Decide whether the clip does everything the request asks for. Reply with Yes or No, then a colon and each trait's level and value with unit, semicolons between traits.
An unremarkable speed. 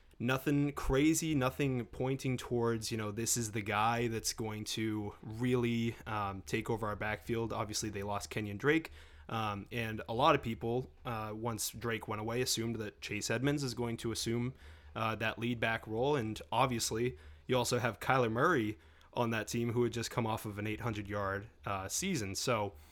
Yes: average, 185 wpm